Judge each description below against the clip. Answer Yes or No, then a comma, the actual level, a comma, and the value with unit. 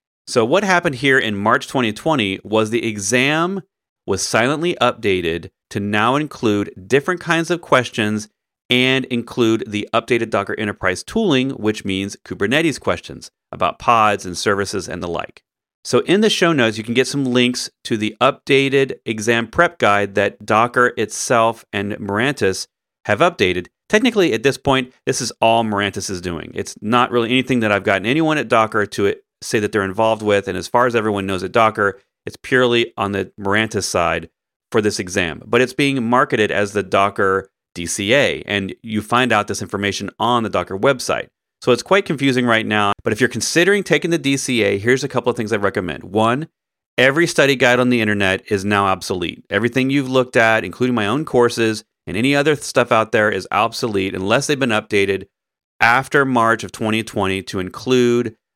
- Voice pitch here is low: Yes, low, 115 Hz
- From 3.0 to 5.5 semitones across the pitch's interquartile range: Yes, average, 4.4 semitones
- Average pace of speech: Yes, average, 185 wpm